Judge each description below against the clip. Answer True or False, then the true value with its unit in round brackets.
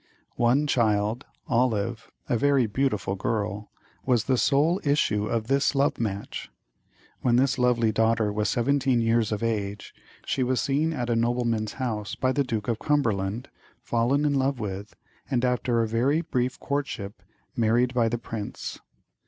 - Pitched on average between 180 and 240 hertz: False (120 Hz)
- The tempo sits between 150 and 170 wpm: True (155 wpm)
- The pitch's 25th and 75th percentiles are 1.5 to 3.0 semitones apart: False (3.5 semitones)